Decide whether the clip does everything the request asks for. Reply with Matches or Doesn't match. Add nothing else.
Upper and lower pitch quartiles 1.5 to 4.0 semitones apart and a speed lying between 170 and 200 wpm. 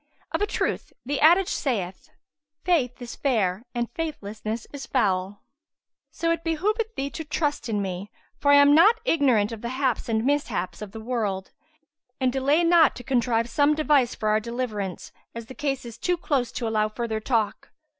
Doesn't match